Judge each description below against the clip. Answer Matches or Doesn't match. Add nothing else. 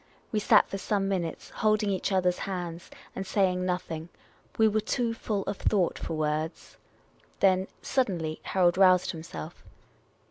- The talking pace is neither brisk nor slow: Matches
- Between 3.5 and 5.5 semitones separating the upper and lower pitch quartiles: Doesn't match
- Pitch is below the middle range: Doesn't match